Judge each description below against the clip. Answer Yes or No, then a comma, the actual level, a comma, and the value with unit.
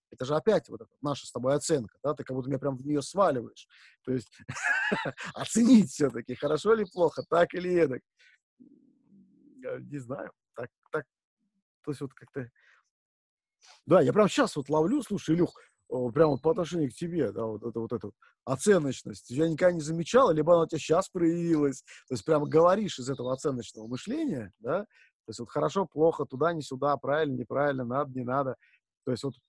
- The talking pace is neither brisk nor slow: No, fast, 185 wpm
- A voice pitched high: No, medium, 150 Hz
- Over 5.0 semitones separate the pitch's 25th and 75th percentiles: Yes, wide, 5.5 semitones